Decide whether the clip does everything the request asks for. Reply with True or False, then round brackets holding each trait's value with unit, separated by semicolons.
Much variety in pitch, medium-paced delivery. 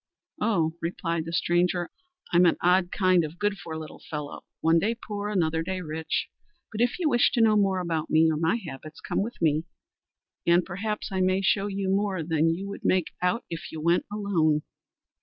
False (3.6 semitones; 195 wpm)